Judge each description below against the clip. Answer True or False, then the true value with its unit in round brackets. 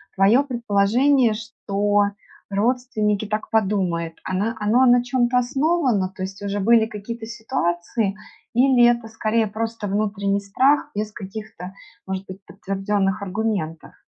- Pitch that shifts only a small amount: False (3.2 semitones)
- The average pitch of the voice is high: True (215 Hz)